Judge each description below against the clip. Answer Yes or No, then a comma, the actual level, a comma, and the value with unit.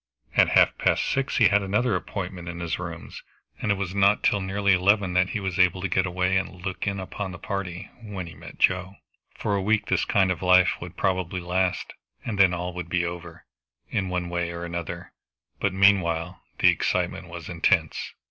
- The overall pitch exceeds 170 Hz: No, very low, 95 Hz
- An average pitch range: No, narrow, 2.0 semitones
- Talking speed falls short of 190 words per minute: No, fast, 205 wpm